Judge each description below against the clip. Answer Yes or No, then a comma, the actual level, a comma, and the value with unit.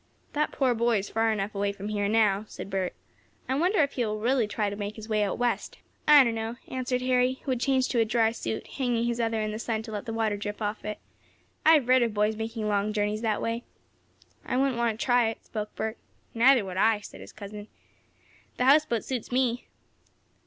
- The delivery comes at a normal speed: No, fast, 230 wpm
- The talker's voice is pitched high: Yes, high, 225 Hz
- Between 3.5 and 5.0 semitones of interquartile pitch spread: No, average, 2.8 semitones